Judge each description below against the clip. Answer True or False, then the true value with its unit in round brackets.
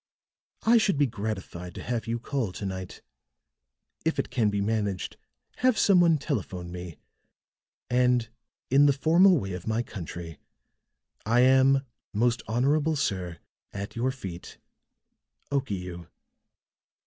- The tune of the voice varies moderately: False (6.5 semitones)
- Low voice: True (115 Hz)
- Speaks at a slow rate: True (130 wpm)